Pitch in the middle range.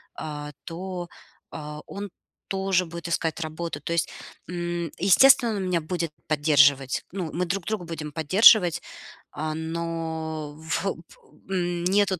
Yes: medium, 170 Hz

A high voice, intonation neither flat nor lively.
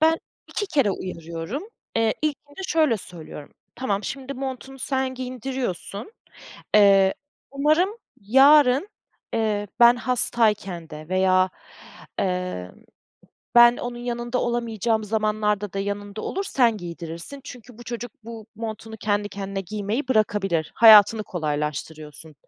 Yes: high, 220 Hz; average, 4.5 semitones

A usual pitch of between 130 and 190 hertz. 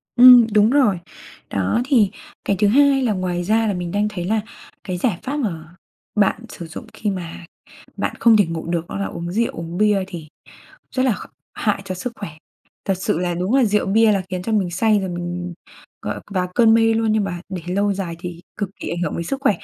No: high, 200 Hz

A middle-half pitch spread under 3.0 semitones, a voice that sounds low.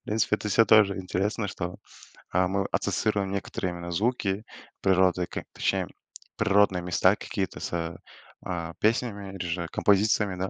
Yes: narrow, 2.6 semitones; very low, 95 Hz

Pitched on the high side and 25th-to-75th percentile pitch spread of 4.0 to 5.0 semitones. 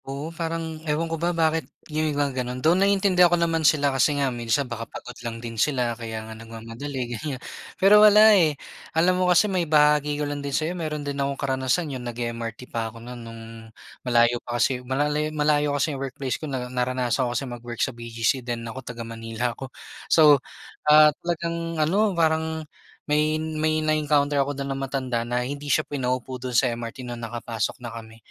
No: medium, 140 Hz; average, 4.5 semitones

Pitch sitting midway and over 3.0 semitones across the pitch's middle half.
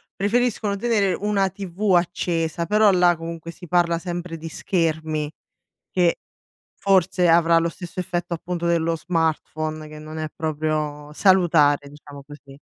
No: medium, 170 Hz; average, 2.7 semitones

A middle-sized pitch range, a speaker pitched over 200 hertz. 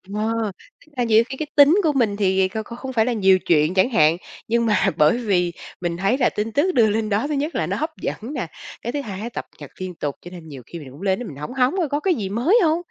No: wide, 6.0 semitones; high, 220 Hz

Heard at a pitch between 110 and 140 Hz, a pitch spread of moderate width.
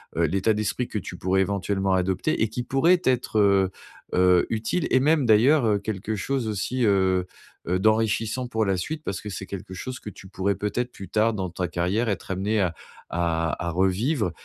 No: low, 100 Hz; average, 3.5 semitones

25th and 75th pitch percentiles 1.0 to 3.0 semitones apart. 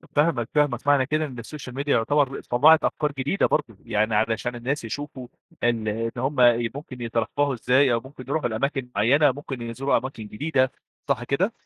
No: average, 3.7 semitones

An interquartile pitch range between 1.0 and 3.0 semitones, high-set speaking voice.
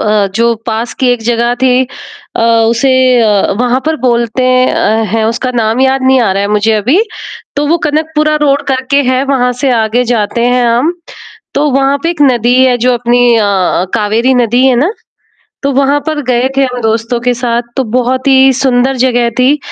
Yes: narrow, 2.5 semitones; very high, 250 Hz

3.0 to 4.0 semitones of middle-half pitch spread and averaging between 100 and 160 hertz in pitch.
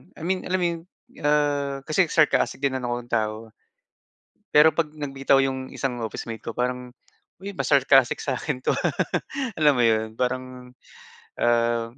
Yes: average, 3.6 semitones; low, 135 Hz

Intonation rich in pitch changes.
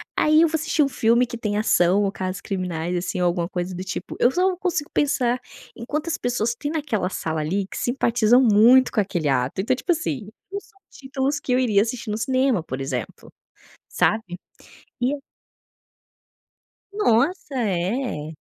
Yes: wide, 6.8 semitones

